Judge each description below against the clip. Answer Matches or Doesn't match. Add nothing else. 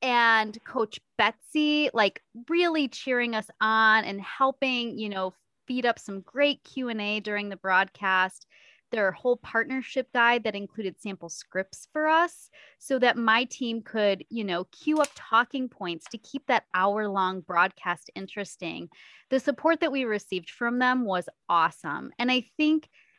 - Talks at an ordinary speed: Matches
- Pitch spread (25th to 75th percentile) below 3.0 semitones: Doesn't match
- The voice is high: Matches